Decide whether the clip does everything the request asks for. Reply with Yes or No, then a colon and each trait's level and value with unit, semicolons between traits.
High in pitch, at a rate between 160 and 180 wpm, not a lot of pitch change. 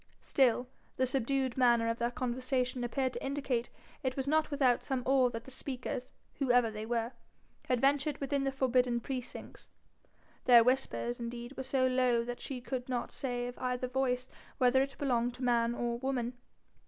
Yes: very high, 250 Hz; average, 175 wpm; narrow, 1.7 semitones